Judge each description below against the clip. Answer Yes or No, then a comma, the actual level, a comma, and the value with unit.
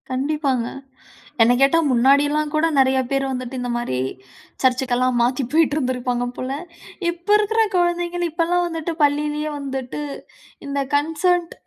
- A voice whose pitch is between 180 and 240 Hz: No, very high, 285 Hz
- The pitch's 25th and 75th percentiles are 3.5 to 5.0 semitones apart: Yes, average, 4.3 semitones